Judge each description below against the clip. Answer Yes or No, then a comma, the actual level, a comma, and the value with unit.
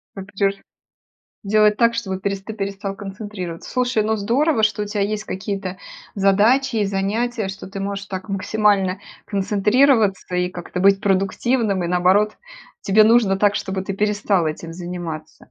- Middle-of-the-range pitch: No, high, 200 Hz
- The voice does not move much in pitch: Yes, narrow, 1.9 semitones